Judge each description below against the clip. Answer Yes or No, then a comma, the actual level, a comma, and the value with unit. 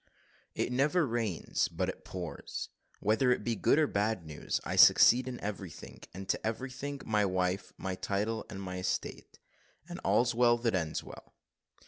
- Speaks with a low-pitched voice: Yes, low, 110 Hz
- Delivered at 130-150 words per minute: No, average, 160 wpm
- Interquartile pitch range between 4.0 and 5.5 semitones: Yes, average, 4.7 semitones